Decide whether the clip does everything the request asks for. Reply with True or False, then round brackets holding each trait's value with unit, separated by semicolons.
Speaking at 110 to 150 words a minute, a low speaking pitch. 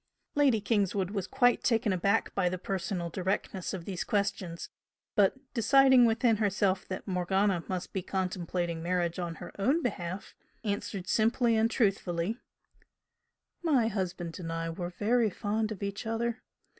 False (145 wpm; 200 Hz)